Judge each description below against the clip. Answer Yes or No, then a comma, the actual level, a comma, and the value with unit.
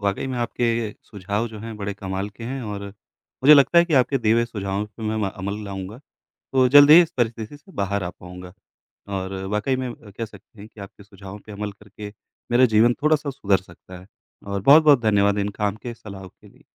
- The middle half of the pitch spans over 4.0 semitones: No, average, 3.3 semitones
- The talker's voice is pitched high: No, low, 105 Hz